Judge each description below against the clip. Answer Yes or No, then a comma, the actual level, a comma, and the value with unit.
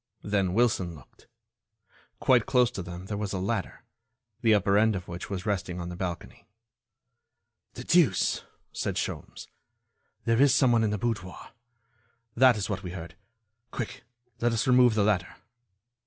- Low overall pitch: Yes, low, 100 Hz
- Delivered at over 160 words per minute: No, average, 155 wpm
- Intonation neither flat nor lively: Yes, average, 4.0 semitones